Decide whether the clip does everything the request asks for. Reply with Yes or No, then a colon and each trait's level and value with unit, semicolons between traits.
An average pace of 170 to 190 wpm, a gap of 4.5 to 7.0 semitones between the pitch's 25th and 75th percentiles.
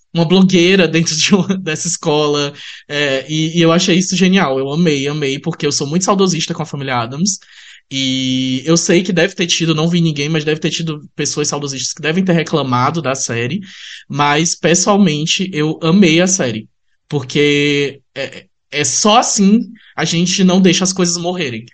No: average, 180 wpm; average, 3.6 semitones